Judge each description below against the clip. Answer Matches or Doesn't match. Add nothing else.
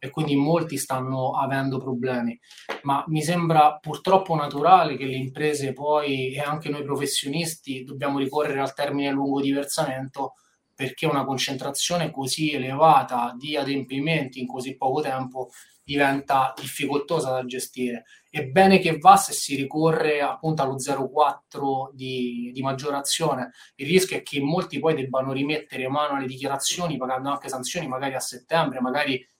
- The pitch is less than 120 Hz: Doesn't match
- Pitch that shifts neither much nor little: Doesn't match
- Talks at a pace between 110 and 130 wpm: Doesn't match